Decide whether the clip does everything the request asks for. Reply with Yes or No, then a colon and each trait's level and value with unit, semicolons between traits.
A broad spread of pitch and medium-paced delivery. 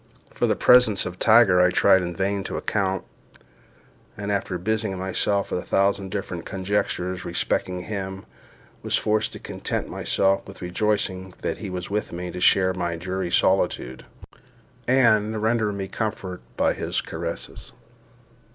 No: narrow, 2.6 semitones; average, 150 wpm